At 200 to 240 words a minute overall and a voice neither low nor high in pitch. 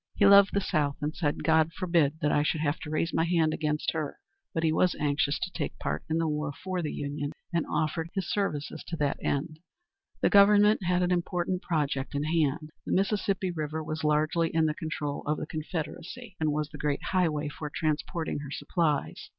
Yes: fast, 205 wpm; medium, 155 Hz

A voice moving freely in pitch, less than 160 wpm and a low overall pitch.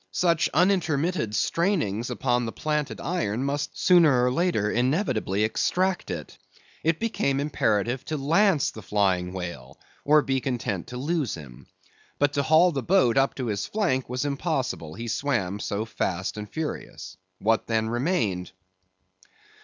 Yes: wide, 7.0 semitones; average, 145 wpm; low, 130 Hz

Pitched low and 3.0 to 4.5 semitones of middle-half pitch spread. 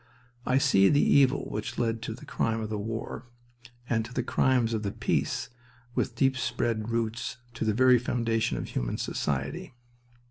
No: low, 115 Hz; narrow, 2.4 semitones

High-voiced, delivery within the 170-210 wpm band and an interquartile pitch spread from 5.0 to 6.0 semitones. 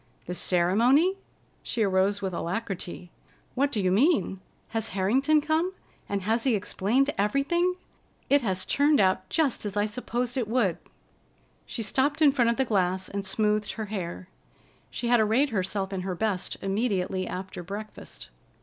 No: high, 210 Hz; average, 160 wpm; wide, 5.4 semitones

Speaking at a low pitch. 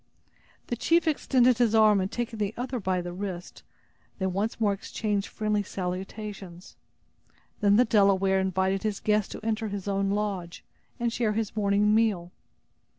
No: high, 205 Hz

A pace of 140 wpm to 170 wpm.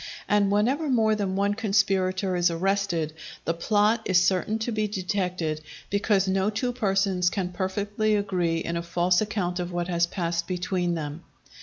Yes: average, 165 wpm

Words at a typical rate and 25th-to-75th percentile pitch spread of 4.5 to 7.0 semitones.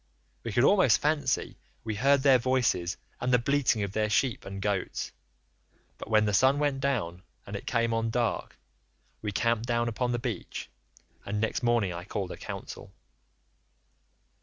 No: average, 165 wpm; average, 3.8 semitones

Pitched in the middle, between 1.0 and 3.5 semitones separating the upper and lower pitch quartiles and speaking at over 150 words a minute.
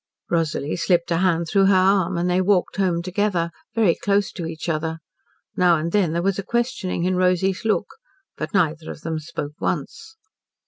Yes: medium, 180 Hz; narrow, 2.6 semitones; average, 185 wpm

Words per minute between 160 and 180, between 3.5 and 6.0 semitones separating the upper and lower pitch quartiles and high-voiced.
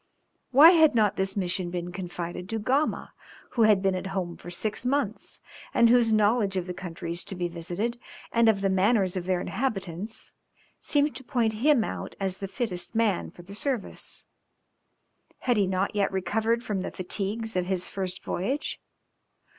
Yes: average, 175 wpm; average, 3.9 semitones; high, 200 Hz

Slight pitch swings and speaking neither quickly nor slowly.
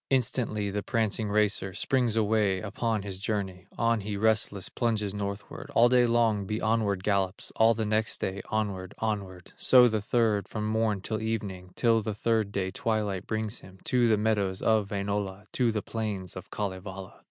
Yes: narrow, 2.1 semitones; average, 175 wpm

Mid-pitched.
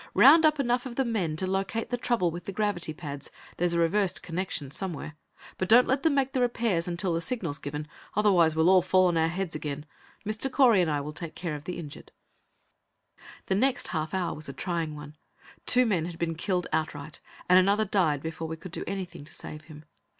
Yes: medium, 175 Hz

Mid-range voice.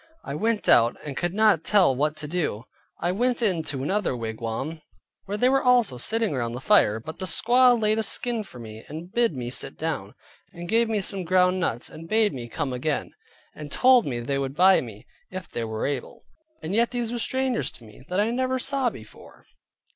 Yes: medium, 175 Hz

